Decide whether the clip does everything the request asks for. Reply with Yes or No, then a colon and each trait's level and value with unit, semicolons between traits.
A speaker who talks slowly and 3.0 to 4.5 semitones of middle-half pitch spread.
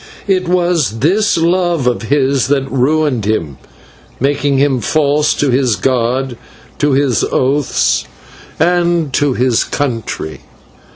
Yes: slow, 120 wpm; average, 3.9 semitones